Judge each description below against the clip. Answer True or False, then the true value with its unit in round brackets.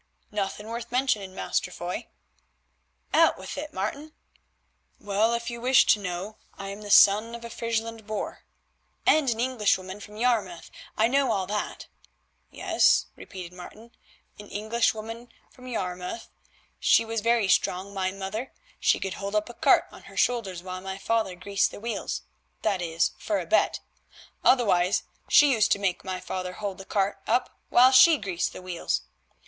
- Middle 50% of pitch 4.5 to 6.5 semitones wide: False (3.6 semitones)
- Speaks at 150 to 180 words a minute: True (165 wpm)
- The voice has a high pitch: True (210 Hz)